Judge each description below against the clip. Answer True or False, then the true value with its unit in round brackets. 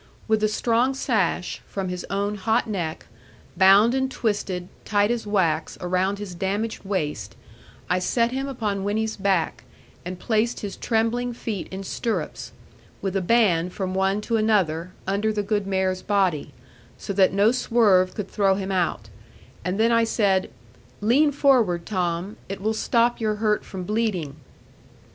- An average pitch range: True (3.1 semitones)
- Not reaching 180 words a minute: True (155 wpm)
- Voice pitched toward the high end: True (200 Hz)